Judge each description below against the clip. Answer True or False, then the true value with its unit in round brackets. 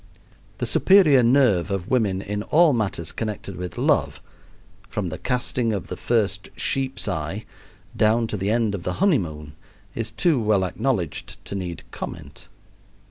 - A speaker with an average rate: True (150 wpm)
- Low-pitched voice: True (105 Hz)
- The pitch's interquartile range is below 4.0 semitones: False (4.8 semitones)